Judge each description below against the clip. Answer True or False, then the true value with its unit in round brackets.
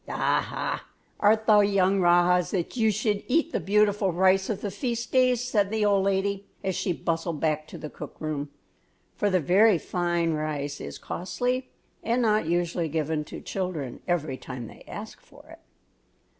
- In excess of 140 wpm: True (170 wpm)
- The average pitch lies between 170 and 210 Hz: True (190 Hz)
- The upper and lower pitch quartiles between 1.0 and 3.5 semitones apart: False (4.2 semitones)